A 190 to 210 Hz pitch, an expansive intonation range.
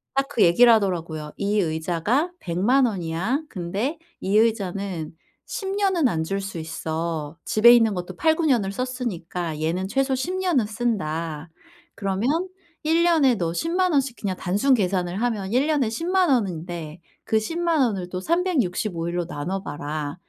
Yes: high, 205 Hz; wide, 7.7 semitones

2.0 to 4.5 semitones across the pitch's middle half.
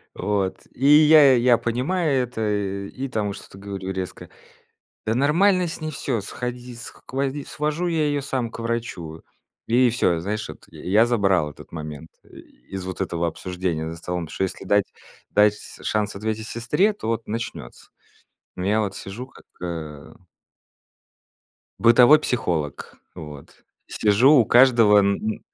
No: average, 5.3 semitones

